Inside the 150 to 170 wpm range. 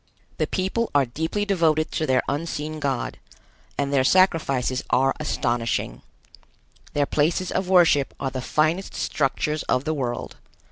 No: average, 140 wpm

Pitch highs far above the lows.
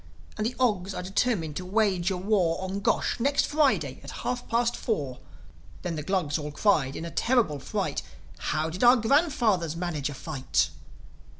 Yes: wide, 6.4 semitones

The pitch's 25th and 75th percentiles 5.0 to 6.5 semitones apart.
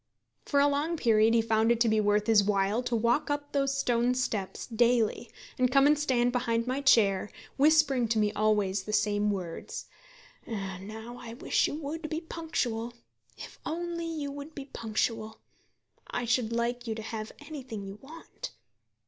No: average, 4.5 semitones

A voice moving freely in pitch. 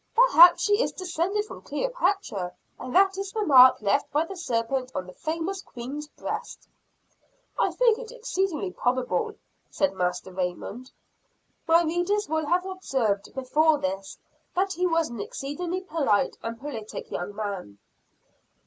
Yes: wide, 8.1 semitones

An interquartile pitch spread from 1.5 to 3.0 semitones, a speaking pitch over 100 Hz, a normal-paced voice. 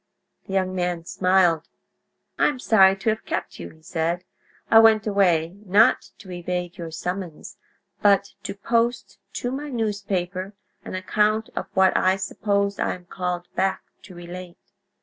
Yes: narrow, 2.6 semitones; high, 190 Hz; average, 155 wpm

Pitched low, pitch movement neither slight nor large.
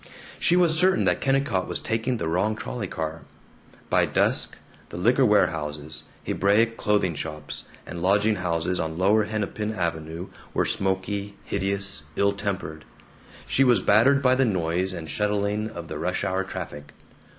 Yes: low, 100 Hz; average, 4.3 semitones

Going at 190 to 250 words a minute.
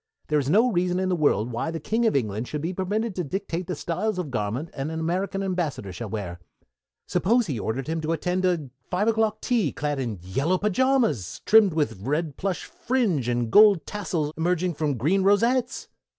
Yes: average, 195 wpm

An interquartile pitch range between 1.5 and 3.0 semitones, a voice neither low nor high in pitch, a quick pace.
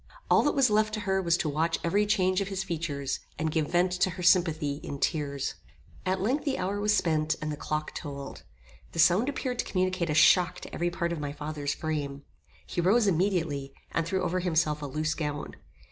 No: average, 3.7 semitones; medium, 170 Hz; fast, 210 wpm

